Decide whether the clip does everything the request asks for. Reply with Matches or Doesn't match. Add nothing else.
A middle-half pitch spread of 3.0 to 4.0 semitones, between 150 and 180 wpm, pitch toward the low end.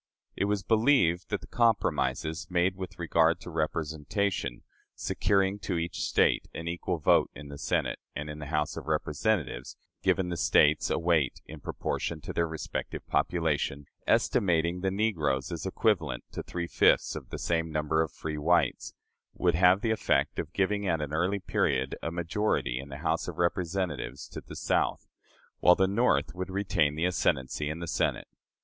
Matches